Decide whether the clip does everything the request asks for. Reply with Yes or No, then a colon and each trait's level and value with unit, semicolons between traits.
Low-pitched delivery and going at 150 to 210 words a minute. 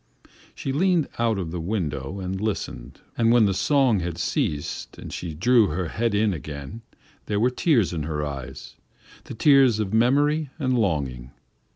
Yes: low, 105 Hz; average, 170 wpm